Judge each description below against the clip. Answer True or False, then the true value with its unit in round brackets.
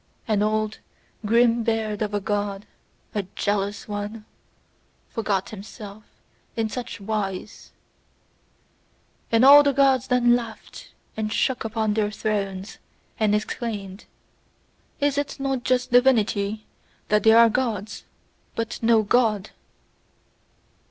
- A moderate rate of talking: False (115 wpm)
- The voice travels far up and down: False (2.5 semitones)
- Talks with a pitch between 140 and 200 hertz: False (220 Hz)